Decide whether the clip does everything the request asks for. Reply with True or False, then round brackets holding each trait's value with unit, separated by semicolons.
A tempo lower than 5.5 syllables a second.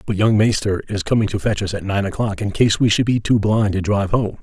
False (6.0 syllables/s)